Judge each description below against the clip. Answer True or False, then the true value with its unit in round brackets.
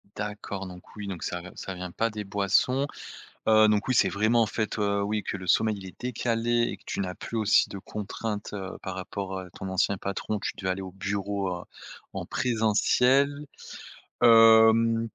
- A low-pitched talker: True (105 Hz)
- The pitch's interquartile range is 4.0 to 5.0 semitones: False (2.9 semitones)